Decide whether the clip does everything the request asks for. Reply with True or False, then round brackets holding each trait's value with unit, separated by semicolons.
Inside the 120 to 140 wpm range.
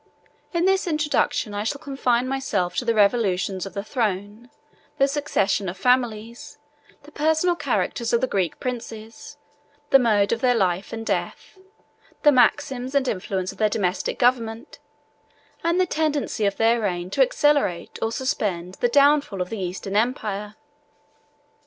False (150 wpm)